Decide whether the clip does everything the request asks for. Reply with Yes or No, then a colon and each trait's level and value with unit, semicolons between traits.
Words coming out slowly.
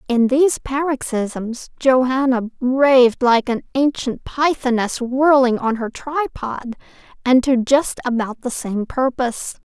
Yes: slow, 125 wpm